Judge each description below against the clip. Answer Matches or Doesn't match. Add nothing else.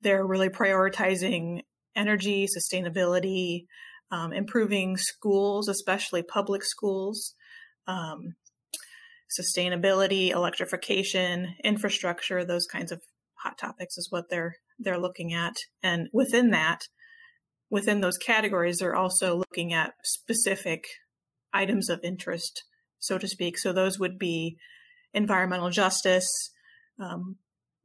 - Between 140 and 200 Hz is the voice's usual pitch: Matches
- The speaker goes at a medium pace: Doesn't match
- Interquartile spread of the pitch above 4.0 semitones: Doesn't match